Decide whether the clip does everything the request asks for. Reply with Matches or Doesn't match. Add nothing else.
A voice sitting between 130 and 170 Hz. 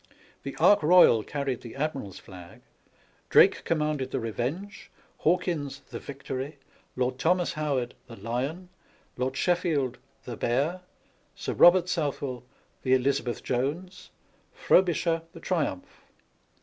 Matches